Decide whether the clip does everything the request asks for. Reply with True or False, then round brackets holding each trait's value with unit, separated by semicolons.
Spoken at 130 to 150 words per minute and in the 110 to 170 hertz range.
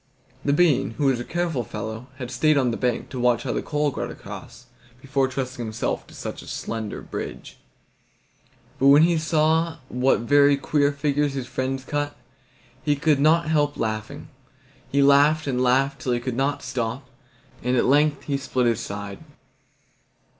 False (175 wpm; 135 Hz)